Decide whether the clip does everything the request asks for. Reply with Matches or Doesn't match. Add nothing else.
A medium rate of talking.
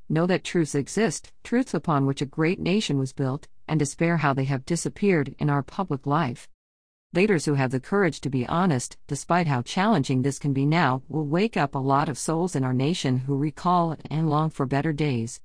Doesn't match